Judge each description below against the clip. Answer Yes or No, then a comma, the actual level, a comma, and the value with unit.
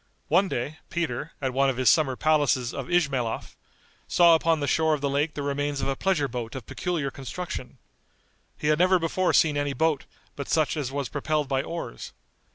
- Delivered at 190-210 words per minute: Yes, average, 195 wpm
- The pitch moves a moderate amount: Yes, average, 3.2 semitones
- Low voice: No, medium, 145 Hz